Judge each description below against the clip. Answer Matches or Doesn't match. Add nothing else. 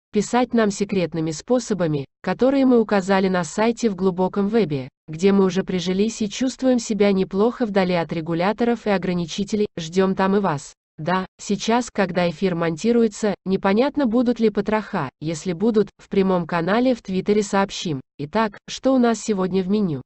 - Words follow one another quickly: Matches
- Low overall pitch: Doesn't match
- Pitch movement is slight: Doesn't match